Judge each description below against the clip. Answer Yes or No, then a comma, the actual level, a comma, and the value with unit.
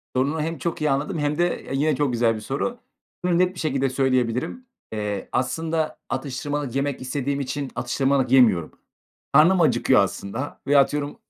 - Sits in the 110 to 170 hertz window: Yes, medium, 140 Hz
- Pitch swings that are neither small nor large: Yes, average, 3.3 semitones